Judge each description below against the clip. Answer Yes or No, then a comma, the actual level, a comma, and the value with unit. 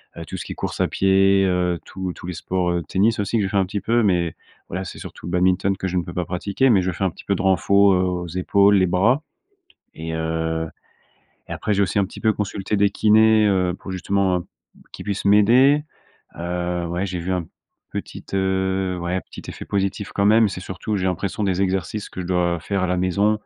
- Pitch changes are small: Yes, narrow, 2.0 semitones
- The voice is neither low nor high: No, very low, 95 Hz